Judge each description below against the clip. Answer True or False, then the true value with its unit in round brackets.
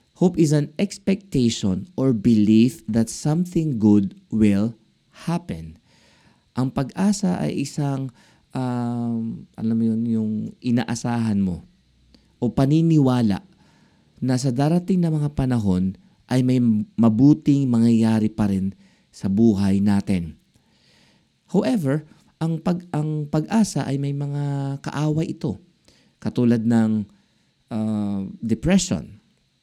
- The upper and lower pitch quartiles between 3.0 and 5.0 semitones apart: False (5.4 semitones)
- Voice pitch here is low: True (125 Hz)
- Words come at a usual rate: False (105 wpm)